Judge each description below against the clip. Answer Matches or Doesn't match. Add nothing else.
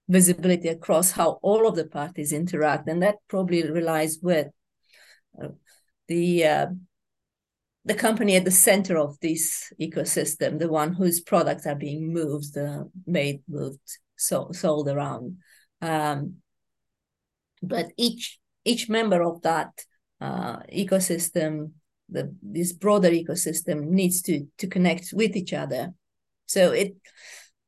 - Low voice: Doesn't match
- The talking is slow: Matches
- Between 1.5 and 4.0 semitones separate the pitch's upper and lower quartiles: Matches